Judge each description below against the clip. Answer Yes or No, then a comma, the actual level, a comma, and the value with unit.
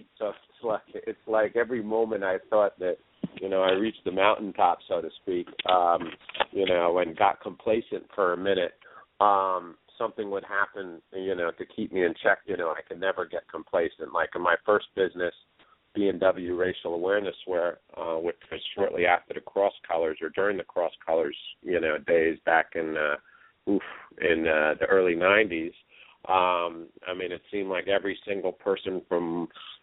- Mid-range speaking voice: No, low, 100 Hz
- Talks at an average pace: Yes, average, 185 wpm